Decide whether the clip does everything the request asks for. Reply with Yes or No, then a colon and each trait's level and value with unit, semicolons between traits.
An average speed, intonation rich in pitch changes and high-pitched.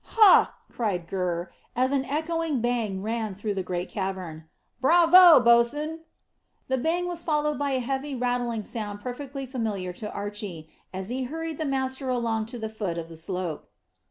Yes: average, 165 wpm; wide, 6.1 semitones; high, 235 Hz